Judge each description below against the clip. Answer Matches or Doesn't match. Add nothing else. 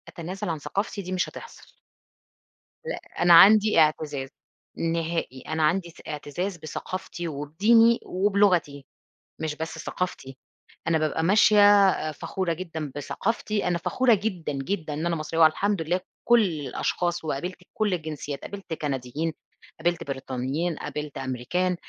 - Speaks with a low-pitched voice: Doesn't match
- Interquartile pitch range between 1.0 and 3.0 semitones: Doesn't match